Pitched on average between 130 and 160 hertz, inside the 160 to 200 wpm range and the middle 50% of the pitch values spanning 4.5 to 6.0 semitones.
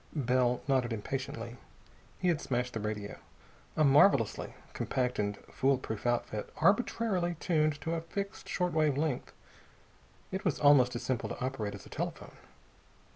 No: low, 135 Hz; average, 145 wpm; average, 5.1 semitones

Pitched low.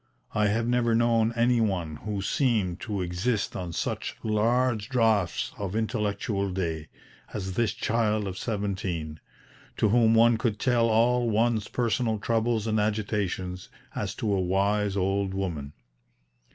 Yes: low, 105 Hz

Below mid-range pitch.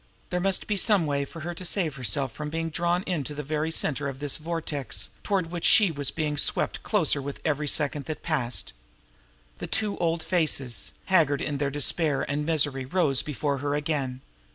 No: medium, 150 Hz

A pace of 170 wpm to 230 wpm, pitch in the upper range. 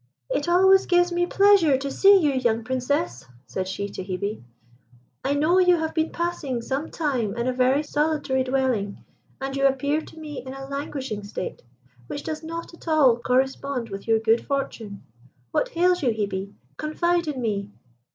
Yes: average, 175 wpm; very high, 270 Hz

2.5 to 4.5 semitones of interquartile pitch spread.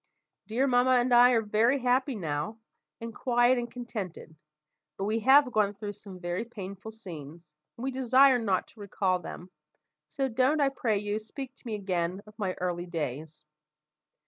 No: average, 5.1 semitones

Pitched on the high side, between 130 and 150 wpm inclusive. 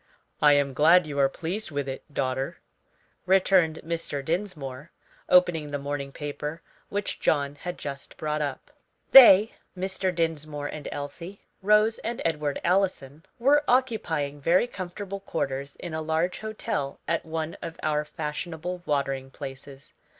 No: medium, 160 Hz; average, 140 wpm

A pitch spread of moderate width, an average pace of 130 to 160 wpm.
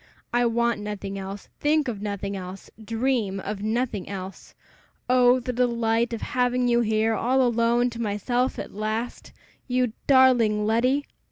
Yes: average, 3.0 semitones; average, 150 wpm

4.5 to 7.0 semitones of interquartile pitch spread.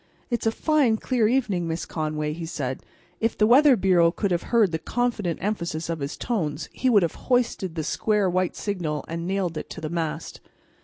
Yes: wide, 5.4 semitones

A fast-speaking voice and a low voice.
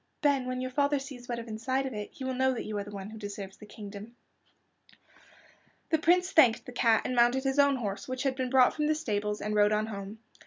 No: fast, 245 wpm; high, 245 Hz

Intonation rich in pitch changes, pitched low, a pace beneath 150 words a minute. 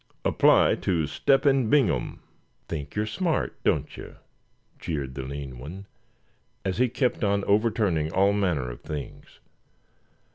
Yes: wide, 7.2 semitones; very low, 95 Hz; slow, 135 wpm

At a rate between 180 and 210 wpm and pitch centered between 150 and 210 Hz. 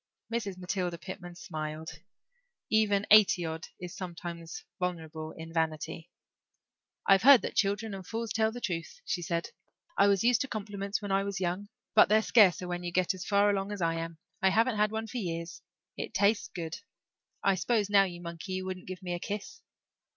Yes: average, 190 wpm; medium, 185 Hz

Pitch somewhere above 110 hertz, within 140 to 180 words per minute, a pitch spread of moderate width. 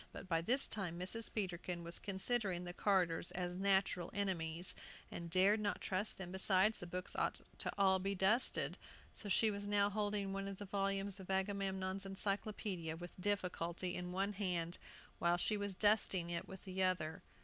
No: high, 190 Hz; average, 175 wpm; narrow, 2.2 semitones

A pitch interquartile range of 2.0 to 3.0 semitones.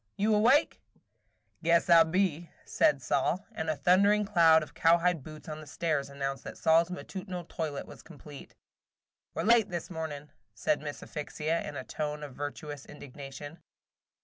No: average, 3.4 semitones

